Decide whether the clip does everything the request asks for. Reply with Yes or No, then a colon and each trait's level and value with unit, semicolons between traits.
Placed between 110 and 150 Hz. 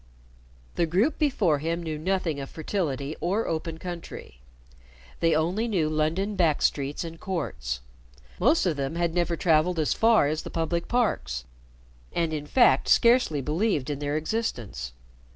No: medium, 165 Hz